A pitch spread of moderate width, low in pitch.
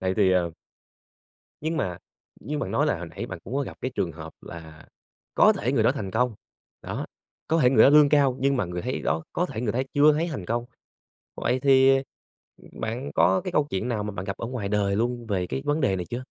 No: wide, 6.4 semitones; low, 120 Hz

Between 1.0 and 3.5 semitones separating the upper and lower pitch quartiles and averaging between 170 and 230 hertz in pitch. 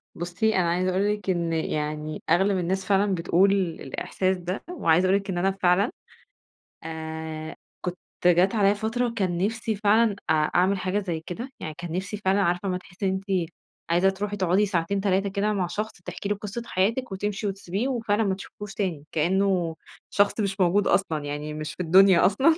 Yes: average, 2.8 semitones; high, 190 Hz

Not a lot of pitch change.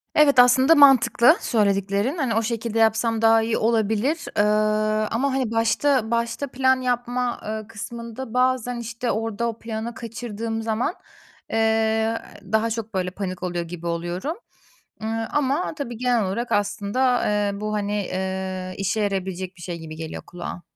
No: average, 3.1 semitones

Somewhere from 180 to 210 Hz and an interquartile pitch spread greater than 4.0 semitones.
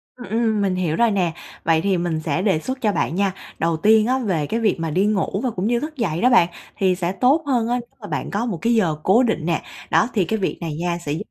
Yes: high, 195 Hz; average, 5.2 semitones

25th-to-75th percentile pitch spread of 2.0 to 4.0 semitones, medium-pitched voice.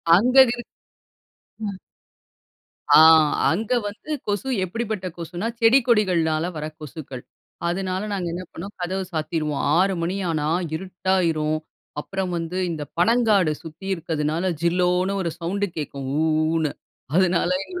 Yes: average, 3.7 semitones; medium, 180 Hz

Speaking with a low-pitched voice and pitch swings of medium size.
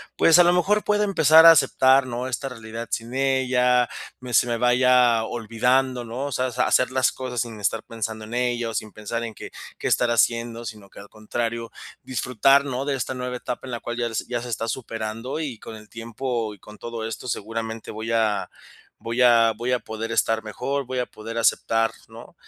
No: low, 120 Hz; narrow, 2.3 semitones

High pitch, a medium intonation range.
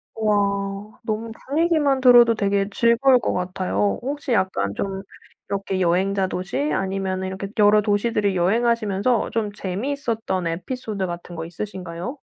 Yes: high, 200 Hz; average, 3.7 semitones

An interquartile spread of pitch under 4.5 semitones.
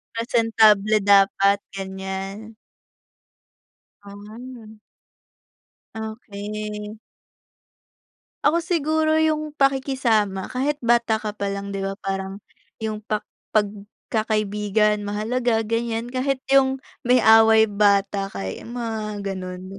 Yes: average, 2.9 semitones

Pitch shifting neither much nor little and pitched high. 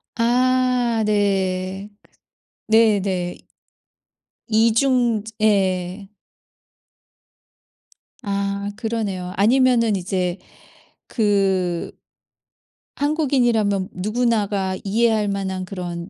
Yes: average, 3.4 semitones; high, 205 Hz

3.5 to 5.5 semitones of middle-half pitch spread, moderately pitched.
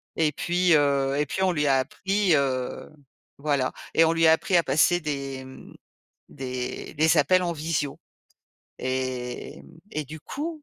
Yes: average, 3.8 semitones; medium, 150 Hz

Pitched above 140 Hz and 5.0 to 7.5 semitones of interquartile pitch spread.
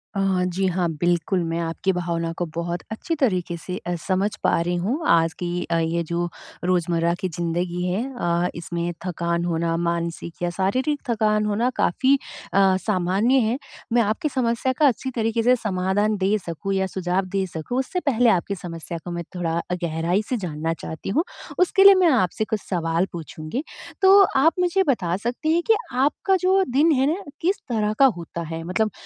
Yes: medium, 185 Hz; wide, 5.6 semitones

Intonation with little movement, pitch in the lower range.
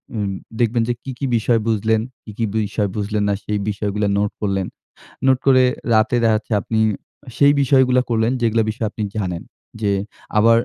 Yes: narrow, 2.2 semitones; low, 110 Hz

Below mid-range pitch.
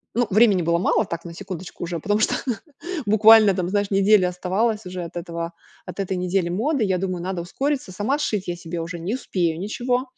No: high, 190 Hz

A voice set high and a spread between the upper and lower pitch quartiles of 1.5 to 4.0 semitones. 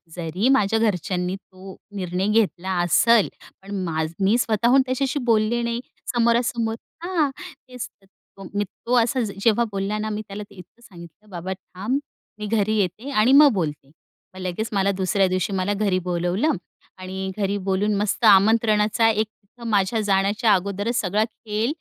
Yes: high, 205 Hz; average, 3.3 semitones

